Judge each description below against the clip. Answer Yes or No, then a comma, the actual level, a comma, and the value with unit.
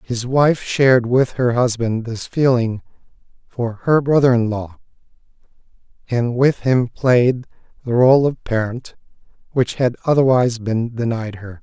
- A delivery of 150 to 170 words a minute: No, average, 140 wpm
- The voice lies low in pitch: Yes, low, 120 Hz